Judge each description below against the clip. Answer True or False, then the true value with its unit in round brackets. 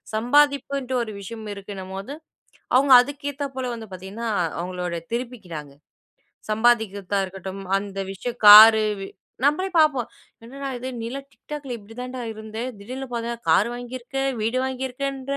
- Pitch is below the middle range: False (235 Hz)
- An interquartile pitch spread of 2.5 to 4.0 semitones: False (4.7 semitones)